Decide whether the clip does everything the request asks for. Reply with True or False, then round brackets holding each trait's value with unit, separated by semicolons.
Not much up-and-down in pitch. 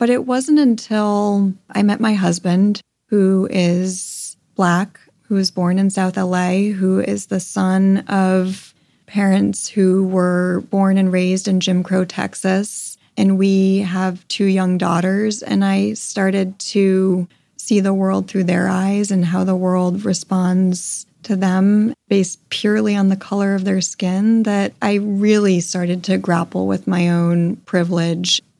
True (1.8 semitones)